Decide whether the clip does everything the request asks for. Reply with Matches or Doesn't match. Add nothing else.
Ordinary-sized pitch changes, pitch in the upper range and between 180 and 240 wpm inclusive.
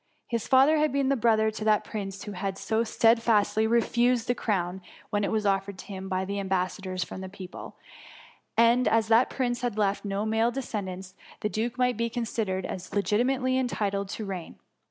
Matches